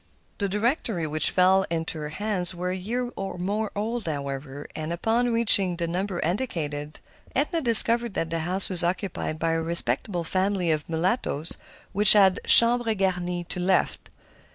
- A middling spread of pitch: Yes, average, 4.2 semitones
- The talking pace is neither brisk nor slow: Yes, average, 160 wpm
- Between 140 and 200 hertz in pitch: Yes, medium, 185 Hz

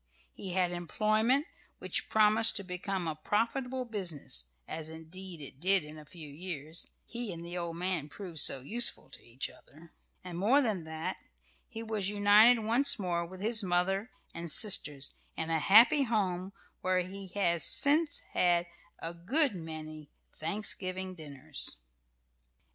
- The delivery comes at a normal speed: Yes, average, 150 wpm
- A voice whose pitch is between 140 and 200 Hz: Yes, medium, 185 Hz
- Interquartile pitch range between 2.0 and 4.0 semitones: No, average, 4.7 semitones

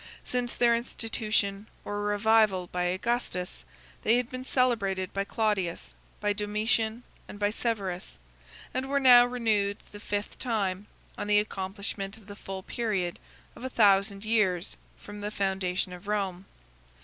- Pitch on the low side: No, high, 205 Hz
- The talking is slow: No, average, 150 wpm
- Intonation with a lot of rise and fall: No, average, 2.7 semitones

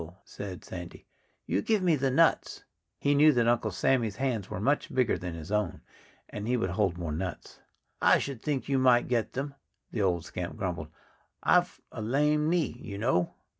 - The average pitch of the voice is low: Yes, low, 115 Hz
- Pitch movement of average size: No, wide, 6.7 semitones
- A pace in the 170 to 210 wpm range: Yes, average, 180 wpm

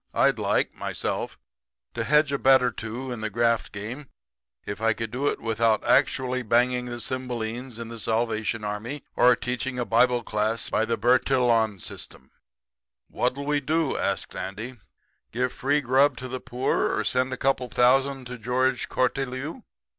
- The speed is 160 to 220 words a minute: Yes, average, 170 wpm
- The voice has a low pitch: Yes, low, 125 Hz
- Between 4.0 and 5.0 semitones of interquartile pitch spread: No, narrow, 2.5 semitones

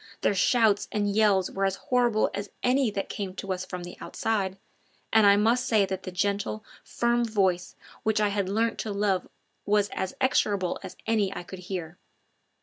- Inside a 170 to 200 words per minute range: Yes, average, 185 wpm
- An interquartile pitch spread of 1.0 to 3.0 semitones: Yes, narrow, 2.5 semitones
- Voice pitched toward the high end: Yes, high, 200 Hz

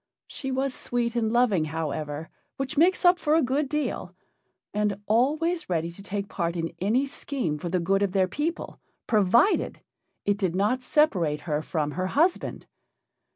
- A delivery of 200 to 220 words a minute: No, average, 165 wpm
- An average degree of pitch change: No, wide, 8.0 semitones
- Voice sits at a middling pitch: No, high, 210 Hz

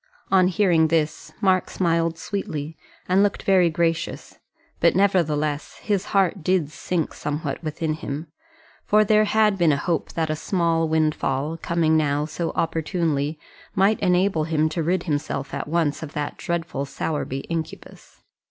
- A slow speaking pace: No, average, 150 wpm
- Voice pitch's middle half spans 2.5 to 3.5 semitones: Yes, average, 3.1 semitones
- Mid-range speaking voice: Yes, medium, 165 Hz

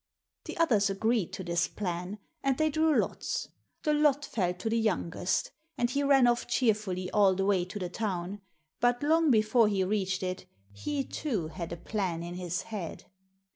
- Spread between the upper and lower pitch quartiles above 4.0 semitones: Yes, average, 5.1 semitones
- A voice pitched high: Yes, high, 205 Hz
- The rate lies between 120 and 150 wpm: No, average, 180 wpm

